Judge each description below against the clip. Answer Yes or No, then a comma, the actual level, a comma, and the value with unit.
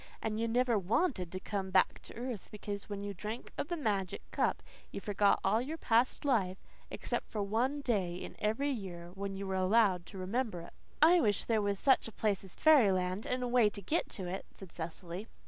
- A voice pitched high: Yes, high, 205 Hz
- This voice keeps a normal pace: No, fast, 215 wpm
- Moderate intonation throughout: Yes, average, 4.0 semitones